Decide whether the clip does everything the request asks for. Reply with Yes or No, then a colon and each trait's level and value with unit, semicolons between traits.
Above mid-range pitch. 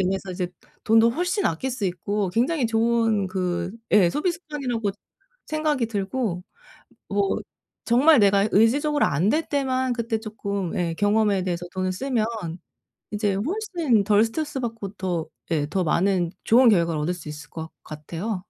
Yes: high, 210 Hz